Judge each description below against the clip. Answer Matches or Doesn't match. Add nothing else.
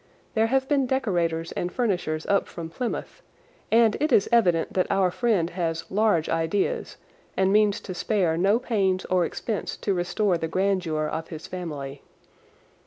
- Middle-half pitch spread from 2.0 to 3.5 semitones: Doesn't match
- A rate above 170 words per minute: Doesn't match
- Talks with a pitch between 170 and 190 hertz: Matches